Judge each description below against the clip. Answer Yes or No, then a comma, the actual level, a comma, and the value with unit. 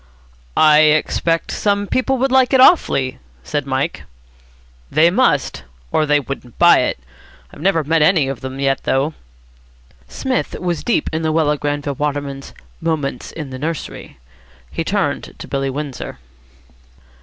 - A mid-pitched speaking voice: Yes, medium, 150 Hz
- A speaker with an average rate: Yes, average, 145 wpm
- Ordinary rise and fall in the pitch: Yes, average, 3.4 semitones